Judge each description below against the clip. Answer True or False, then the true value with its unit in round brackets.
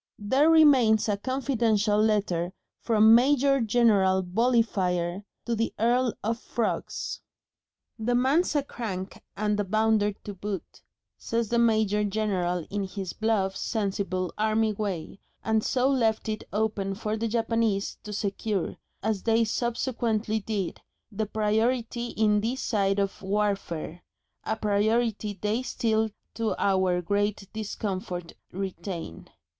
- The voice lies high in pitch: True (215 Hz)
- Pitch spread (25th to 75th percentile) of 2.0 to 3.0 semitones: True (2.6 semitones)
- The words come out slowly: True (130 wpm)